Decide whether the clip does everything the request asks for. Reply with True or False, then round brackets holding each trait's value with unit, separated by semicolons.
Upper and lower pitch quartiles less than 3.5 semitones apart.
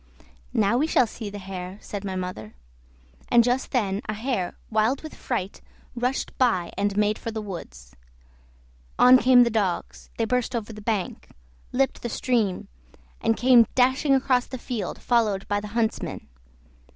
False (3.8 semitones)